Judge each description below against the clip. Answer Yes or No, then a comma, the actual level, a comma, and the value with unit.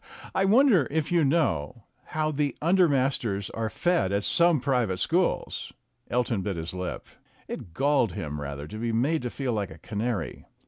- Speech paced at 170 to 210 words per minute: Yes, average, 180 wpm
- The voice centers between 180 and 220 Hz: No, low, 125 Hz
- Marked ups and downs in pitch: Yes, wide, 7.8 semitones